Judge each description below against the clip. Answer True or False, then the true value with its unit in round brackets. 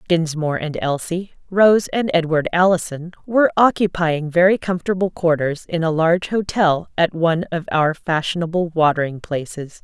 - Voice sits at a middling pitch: True (170 Hz)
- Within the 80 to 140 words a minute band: True (135 wpm)